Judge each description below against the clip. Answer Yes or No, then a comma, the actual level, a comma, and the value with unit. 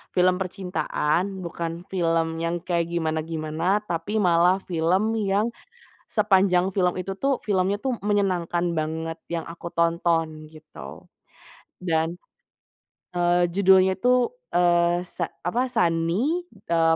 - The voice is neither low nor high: Yes, medium, 175 Hz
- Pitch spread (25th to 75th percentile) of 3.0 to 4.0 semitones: No, narrow, 2.5 semitones